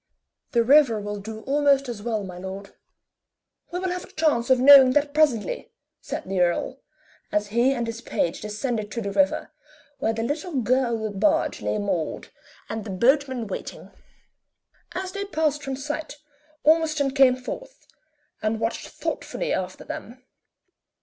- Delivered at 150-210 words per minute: Yes, average, 155 wpm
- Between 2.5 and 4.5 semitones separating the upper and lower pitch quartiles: No, average, 5.3 semitones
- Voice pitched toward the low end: No, very high, 250 Hz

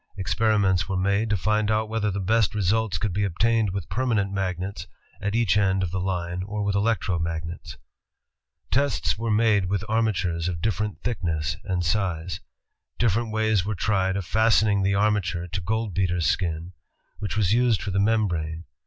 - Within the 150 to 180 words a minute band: Yes, average, 170 wpm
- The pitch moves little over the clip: No, average, 3.2 semitones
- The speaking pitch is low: Yes, low, 100 Hz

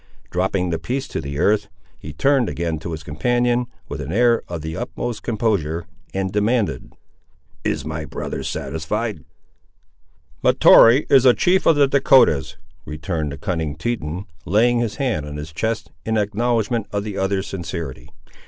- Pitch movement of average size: No, wide, 6.8 semitones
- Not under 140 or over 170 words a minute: Yes, average, 155 wpm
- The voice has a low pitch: Yes, low, 100 Hz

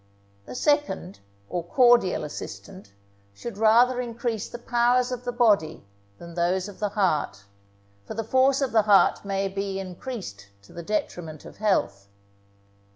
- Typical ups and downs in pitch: No, wide, 5.8 semitones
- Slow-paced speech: No, average, 150 wpm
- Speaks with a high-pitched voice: Yes, high, 200 Hz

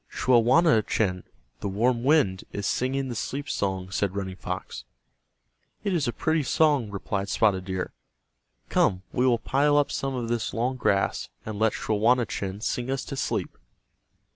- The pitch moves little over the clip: No, average, 5.0 semitones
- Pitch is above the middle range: No, low, 115 Hz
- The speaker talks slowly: No, average, 155 wpm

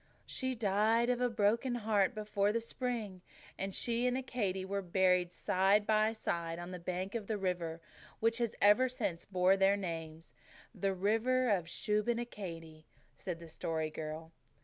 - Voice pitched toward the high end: Yes, high, 200 Hz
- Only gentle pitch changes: No, average, 4.2 semitones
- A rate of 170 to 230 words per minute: No, average, 155 wpm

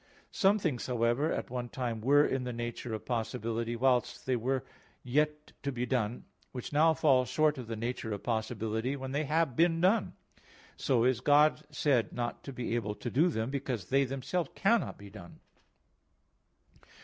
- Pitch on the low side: Yes, low, 125 Hz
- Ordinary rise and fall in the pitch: Yes, average, 3.8 semitones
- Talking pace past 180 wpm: No, average, 175 wpm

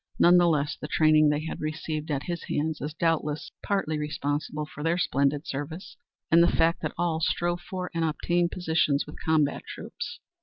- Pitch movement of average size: No, narrow, 2.3 semitones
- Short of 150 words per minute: No, average, 185 wpm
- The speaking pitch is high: No, medium, 155 Hz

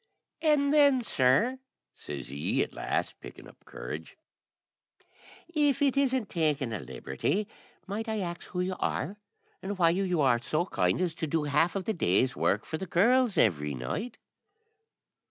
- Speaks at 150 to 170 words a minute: Yes, average, 160 wpm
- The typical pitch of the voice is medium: Yes, medium, 180 Hz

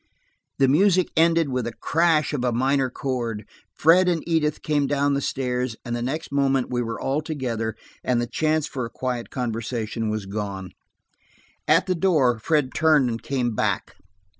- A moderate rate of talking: Yes, average, 175 wpm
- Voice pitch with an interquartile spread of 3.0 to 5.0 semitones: Yes, average, 4.5 semitones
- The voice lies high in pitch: No, low, 130 Hz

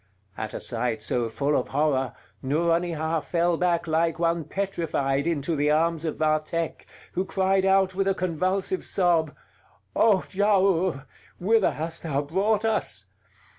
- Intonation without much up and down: No, average, 3.9 semitones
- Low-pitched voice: No, medium, 165 Hz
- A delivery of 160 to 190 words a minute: No, average, 140 wpm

